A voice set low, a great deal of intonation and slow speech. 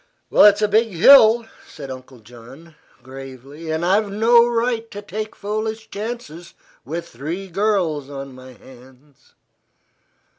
No: medium, 170 Hz; wide, 8.1 semitones; slow, 125 wpm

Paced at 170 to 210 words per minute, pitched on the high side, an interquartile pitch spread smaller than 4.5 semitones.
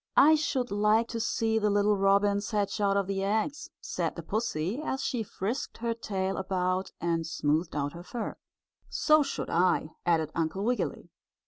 Yes: average, 175 wpm; high, 200 Hz; average, 3.8 semitones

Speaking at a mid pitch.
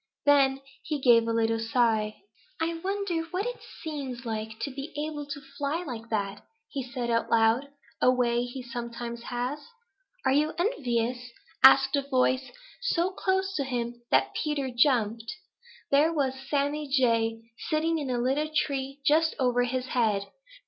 No: very high, 260 Hz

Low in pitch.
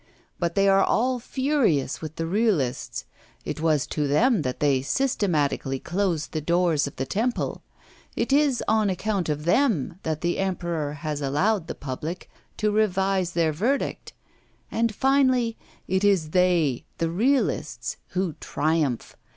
No: medium, 180 Hz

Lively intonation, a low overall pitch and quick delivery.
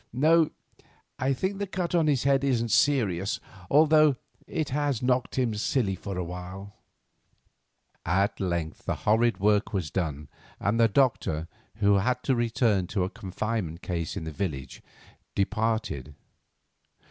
No: wide, 6.2 semitones; low, 110 Hz; average, 145 wpm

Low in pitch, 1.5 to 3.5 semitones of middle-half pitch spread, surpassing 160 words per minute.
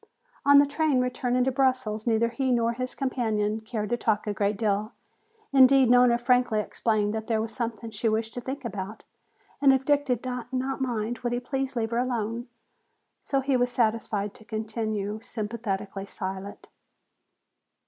No: high, 235 Hz; average, 2.8 semitones; average, 170 wpm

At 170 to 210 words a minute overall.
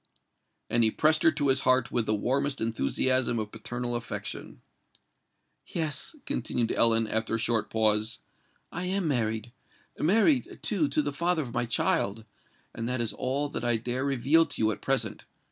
No: average, 160 wpm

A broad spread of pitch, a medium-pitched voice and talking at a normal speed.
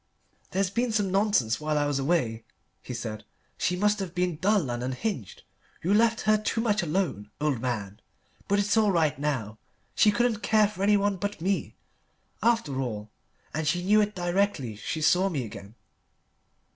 Yes: wide, 7.8 semitones; medium, 180 Hz; average, 170 wpm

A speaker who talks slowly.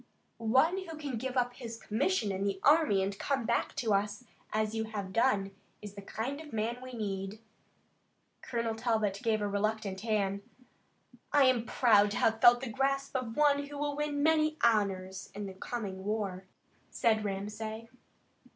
No: average, 170 wpm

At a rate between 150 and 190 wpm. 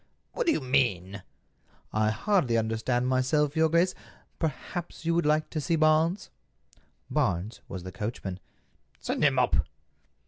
No: average, 140 wpm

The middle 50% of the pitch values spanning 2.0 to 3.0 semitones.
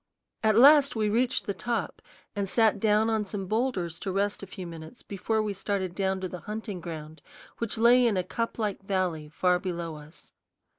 No: average, 3.6 semitones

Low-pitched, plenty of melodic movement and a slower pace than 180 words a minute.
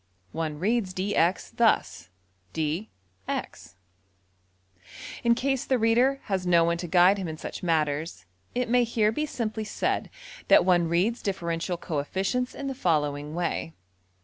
No: medium, 185 Hz; wide, 5.7 semitones; average, 145 wpm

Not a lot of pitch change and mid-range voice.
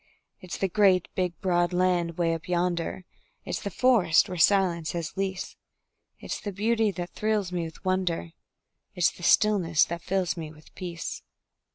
Yes: narrow, 2.2 semitones; medium, 180 Hz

